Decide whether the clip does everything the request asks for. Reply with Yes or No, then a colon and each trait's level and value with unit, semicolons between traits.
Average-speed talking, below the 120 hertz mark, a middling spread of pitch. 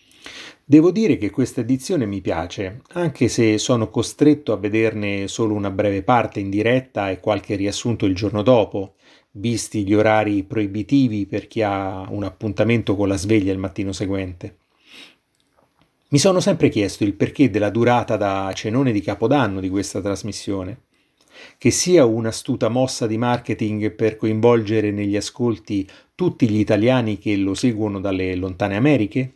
Yes: average, 150 wpm; low, 110 Hz; average, 3.3 semitones